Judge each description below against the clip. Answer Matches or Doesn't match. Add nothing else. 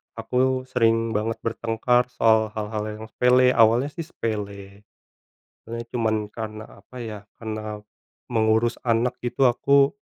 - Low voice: Matches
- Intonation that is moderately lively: Doesn't match